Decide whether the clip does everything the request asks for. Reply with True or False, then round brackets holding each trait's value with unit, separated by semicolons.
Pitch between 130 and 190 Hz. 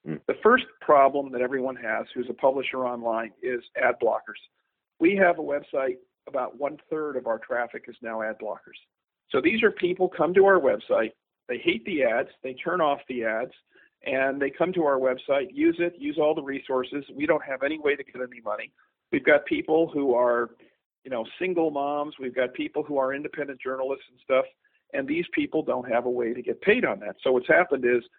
True (140 Hz)